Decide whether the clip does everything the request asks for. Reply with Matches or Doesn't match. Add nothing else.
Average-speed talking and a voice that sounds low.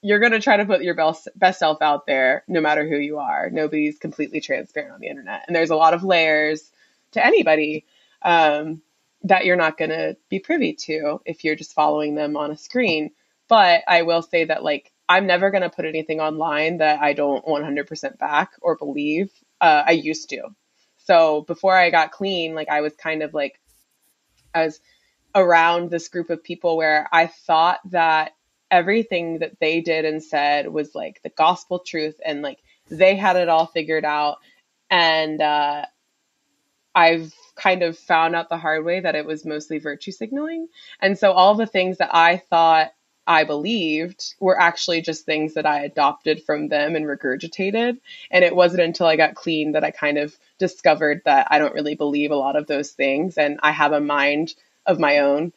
Doesn't match